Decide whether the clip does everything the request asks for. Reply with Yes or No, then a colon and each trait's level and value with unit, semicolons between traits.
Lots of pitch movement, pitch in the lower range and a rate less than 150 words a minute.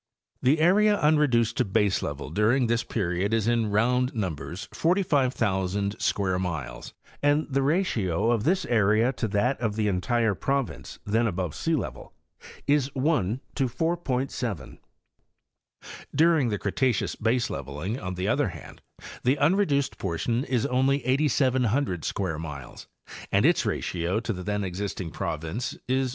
Yes: wide, 6.0 semitones; low, 115 Hz; average, 140 wpm